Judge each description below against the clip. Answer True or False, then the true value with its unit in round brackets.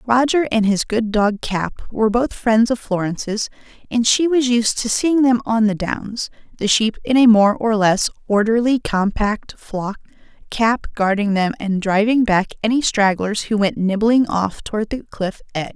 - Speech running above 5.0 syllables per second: False (4.6 syllables/s)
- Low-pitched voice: False (220 Hz)